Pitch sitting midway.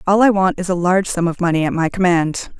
Yes: medium, 180 Hz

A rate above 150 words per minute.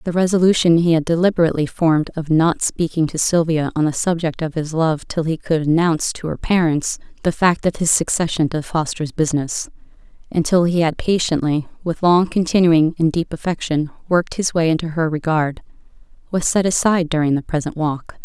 Yes: average, 185 wpm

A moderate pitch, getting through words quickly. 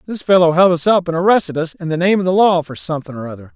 Yes: medium, 170 Hz; fast, 305 wpm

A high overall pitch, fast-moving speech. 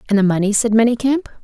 Yes: high, 225 Hz; fast, 210 wpm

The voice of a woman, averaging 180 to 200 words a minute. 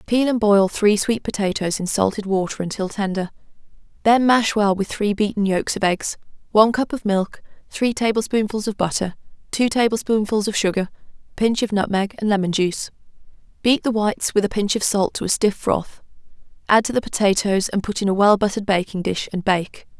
Yes: female; average, 195 wpm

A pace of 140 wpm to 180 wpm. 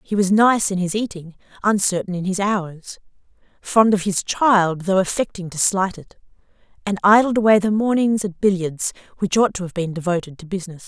No: average, 190 wpm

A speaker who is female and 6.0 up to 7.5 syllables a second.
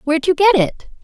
Yes: female; 6.3 syllables/s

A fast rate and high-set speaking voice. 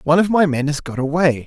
No: fast, 285 wpm; medium, 155 Hz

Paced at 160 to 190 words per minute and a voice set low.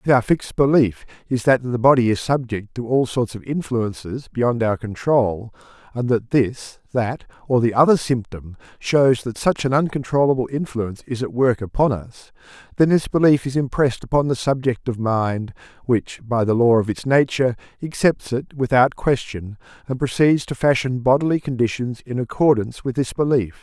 Yes: average, 175 wpm; low, 125 Hz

